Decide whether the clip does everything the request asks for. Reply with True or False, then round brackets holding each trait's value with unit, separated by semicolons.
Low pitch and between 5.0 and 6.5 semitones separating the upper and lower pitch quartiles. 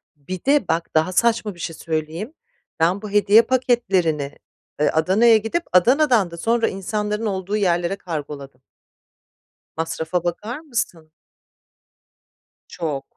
False (185 Hz; 5.5 semitones)